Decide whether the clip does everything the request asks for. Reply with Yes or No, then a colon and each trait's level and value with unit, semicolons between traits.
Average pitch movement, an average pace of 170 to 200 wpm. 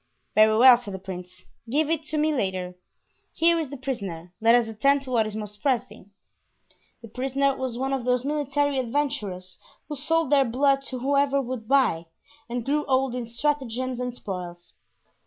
Yes: average, 4.4 semitones; average, 175 wpm